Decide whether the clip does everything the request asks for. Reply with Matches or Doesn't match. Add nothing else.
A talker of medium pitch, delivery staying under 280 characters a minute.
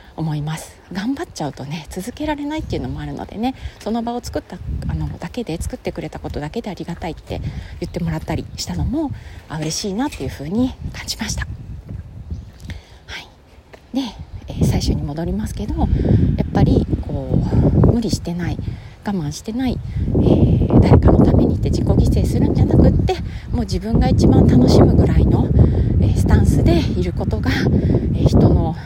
Doesn't match